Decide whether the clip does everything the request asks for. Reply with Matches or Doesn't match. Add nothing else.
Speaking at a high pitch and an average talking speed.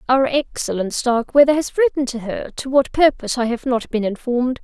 Matches